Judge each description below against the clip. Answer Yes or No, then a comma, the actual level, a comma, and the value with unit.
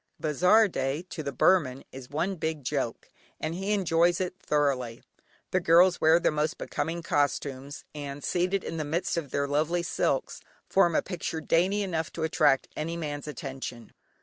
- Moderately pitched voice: Yes, medium, 160 Hz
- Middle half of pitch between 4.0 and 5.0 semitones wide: No, average, 3.5 semitones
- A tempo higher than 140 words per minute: Yes, average, 170 wpm